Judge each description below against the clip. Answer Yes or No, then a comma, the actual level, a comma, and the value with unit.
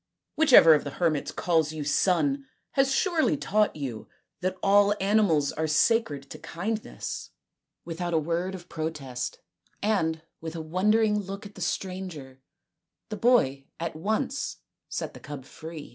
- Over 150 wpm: No, average, 145 wpm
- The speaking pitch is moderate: Yes, medium, 175 Hz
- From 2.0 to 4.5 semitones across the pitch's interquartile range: No, average, 5.3 semitones